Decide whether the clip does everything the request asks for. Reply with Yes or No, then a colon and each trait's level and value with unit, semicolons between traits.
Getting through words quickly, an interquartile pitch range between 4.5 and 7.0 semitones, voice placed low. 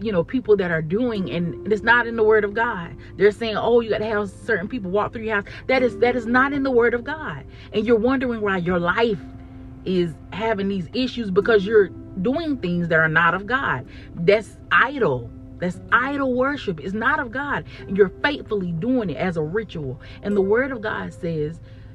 No: fast, 215 wpm; wide, 5.5 semitones; high, 210 Hz